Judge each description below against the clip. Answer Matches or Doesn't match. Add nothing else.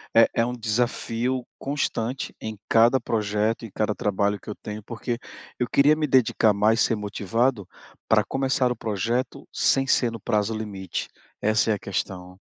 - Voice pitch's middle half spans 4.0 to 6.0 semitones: Doesn't match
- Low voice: Matches